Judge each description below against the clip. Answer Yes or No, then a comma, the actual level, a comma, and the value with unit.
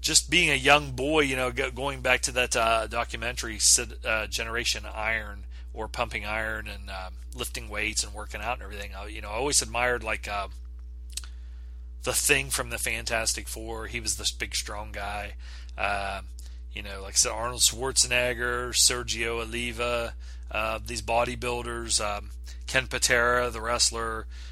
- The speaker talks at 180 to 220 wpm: No, average, 165 wpm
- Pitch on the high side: No, low, 115 Hz